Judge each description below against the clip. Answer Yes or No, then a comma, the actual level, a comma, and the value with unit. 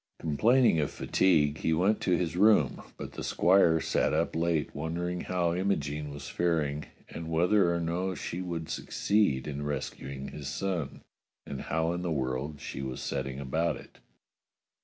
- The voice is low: Yes, very low, 80 Hz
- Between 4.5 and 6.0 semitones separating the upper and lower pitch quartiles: No, average, 3.4 semitones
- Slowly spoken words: No, average, 160 wpm